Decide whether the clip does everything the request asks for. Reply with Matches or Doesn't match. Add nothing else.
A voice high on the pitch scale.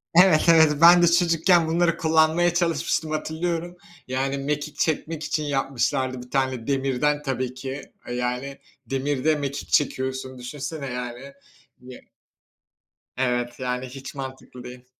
Doesn't match